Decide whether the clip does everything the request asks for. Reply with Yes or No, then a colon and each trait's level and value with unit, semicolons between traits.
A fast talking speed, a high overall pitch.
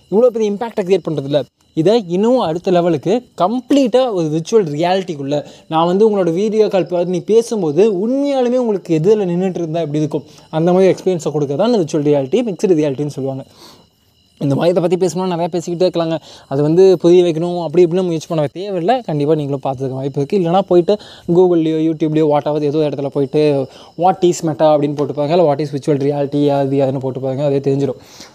No: fast, 180 wpm; medium, 165 Hz